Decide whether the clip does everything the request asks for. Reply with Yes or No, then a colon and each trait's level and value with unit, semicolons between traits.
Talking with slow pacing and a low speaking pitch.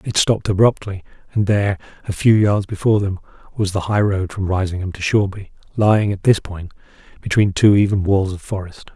No: average, 190 wpm; low, 100 Hz